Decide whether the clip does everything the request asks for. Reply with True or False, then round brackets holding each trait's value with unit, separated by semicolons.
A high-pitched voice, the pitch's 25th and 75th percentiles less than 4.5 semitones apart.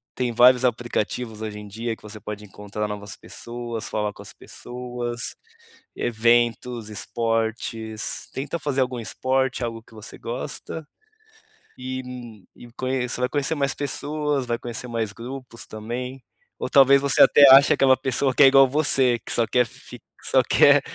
False (120 Hz; 2.7 semitones)